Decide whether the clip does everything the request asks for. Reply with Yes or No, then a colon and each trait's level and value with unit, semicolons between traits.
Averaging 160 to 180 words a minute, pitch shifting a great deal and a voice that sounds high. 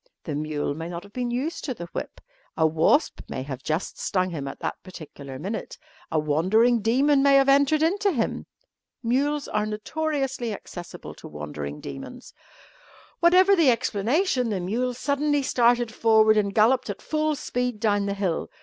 Yes: average, 170 wpm; wide, 7.7 semitones; high, 225 Hz